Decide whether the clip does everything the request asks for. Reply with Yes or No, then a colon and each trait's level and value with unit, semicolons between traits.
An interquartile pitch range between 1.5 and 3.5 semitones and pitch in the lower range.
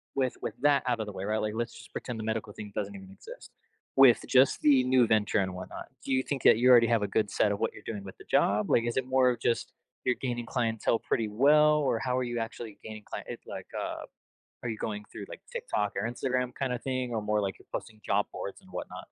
Yes: average, 3.2 semitones; low, 115 Hz